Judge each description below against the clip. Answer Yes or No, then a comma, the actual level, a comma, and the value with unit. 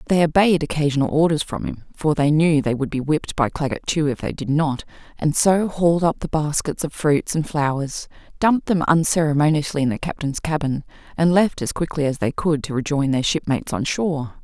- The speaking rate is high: Yes, fast, 210 wpm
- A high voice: No, medium, 155 Hz